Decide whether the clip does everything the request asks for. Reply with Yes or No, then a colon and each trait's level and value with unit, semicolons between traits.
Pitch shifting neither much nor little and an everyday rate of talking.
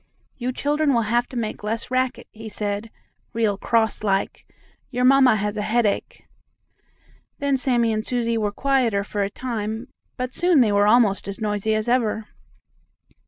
Yes: average, 3.1 semitones; average, 165 wpm